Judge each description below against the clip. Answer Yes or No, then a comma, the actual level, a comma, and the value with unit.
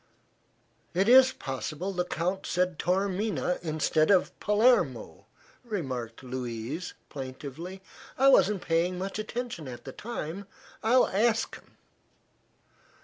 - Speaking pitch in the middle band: Yes, medium, 180 Hz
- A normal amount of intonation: No, wide, 6.5 semitones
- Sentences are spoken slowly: Yes, slow, 110 wpm